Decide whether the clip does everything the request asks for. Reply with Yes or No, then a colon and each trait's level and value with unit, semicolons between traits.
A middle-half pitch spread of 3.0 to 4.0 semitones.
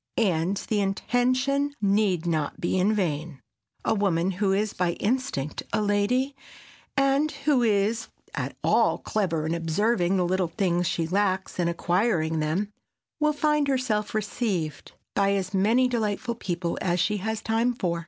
No: average, 5.0 semitones